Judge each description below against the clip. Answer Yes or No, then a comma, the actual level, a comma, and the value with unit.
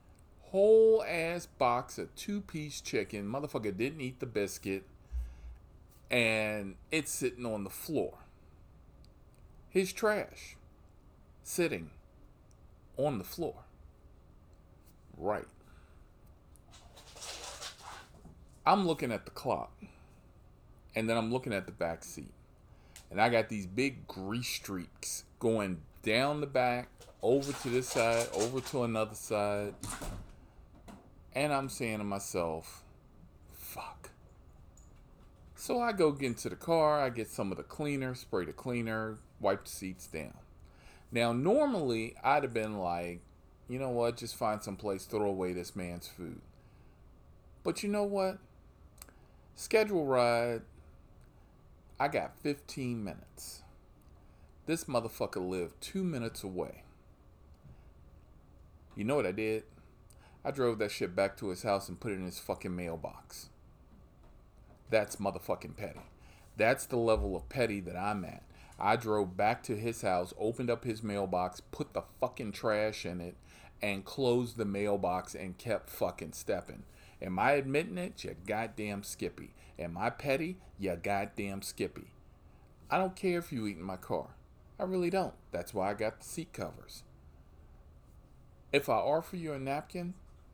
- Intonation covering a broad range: Yes, wide, 6.1 semitones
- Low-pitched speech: Yes, low, 105 Hz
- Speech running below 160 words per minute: Yes, average, 140 wpm